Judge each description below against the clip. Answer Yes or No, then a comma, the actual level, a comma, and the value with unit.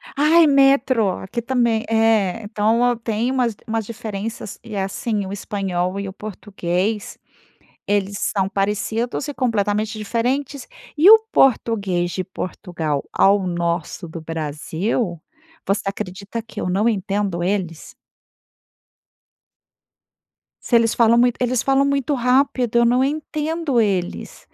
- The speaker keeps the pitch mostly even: No, average, 4.1 semitones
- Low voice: No, high, 215 Hz